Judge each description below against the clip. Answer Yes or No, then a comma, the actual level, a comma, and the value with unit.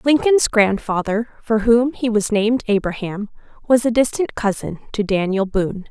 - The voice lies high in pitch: Yes, high, 220 Hz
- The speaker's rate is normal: Yes, average, 150 wpm